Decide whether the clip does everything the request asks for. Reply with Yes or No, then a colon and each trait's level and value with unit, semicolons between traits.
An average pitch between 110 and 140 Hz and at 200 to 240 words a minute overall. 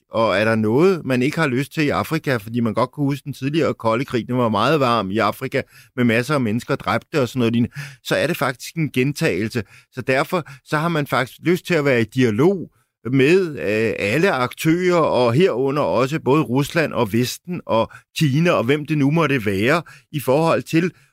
Yes: low, 135 Hz; average, 210 wpm